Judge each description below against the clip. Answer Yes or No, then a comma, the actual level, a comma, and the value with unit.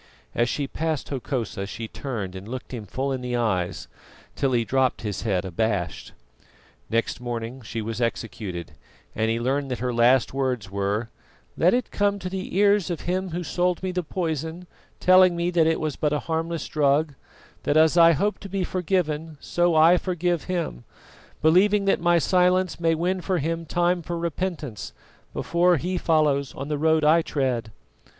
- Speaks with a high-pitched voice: No, medium, 155 Hz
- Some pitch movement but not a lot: No, wide, 6.5 semitones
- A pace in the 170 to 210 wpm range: Yes, average, 180 wpm